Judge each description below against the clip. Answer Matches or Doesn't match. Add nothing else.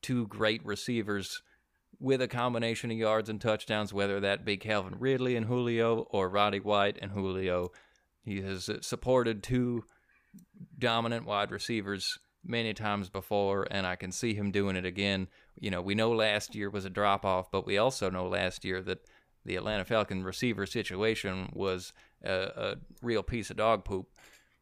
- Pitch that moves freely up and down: Doesn't match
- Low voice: Matches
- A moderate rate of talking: Matches